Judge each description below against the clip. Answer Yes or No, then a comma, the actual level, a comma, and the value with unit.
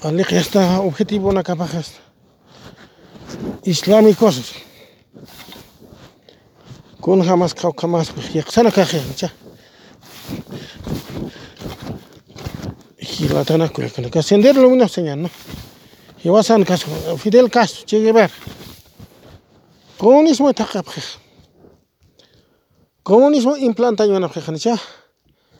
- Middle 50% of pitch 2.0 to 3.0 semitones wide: No, average, 5.1 semitones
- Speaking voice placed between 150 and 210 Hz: Yes, high, 190 Hz